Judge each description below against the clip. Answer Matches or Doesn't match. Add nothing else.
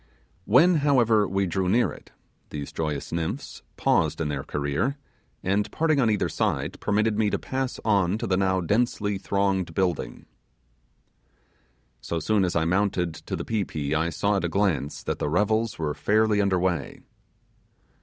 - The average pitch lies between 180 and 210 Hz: Doesn't match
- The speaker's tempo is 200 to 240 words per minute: Doesn't match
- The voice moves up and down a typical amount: Matches